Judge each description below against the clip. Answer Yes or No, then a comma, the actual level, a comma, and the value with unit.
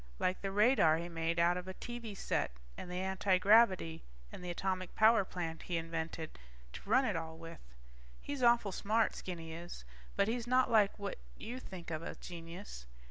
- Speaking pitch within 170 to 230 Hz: Yes, medium, 185 Hz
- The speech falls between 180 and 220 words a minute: Yes, average, 185 wpm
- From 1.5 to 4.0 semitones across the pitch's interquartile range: No, average, 4.5 semitones